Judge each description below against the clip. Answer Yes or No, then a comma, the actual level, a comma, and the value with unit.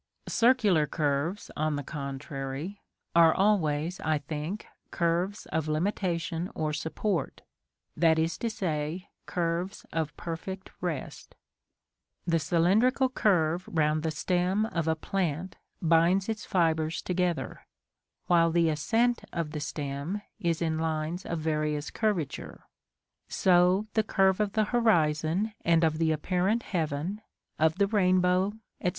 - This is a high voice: No, medium, 170 Hz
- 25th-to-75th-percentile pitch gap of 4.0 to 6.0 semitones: No, average, 3.5 semitones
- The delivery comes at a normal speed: No, slow, 130 wpm